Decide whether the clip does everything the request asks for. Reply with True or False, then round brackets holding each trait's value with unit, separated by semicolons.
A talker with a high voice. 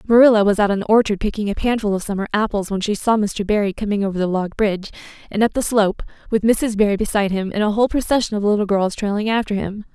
True (210 Hz)